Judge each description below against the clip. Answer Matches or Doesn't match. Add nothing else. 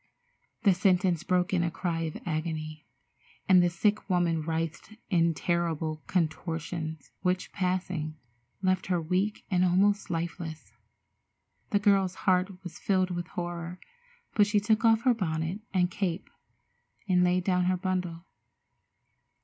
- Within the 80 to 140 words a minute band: Matches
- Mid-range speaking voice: Matches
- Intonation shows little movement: Matches